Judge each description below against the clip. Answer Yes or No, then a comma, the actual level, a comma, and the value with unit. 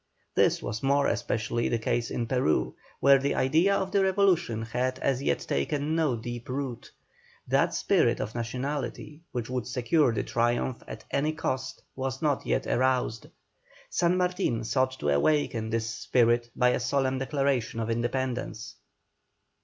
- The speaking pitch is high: No, low, 130 Hz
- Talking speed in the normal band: Yes, average, 155 wpm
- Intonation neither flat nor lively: Yes, average, 3.2 semitones